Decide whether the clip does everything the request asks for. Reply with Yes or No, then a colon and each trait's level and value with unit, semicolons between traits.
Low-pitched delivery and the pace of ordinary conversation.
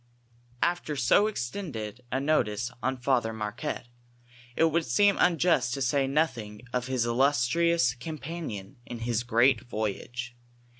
No: low, 125 Hz; slow, 130 wpm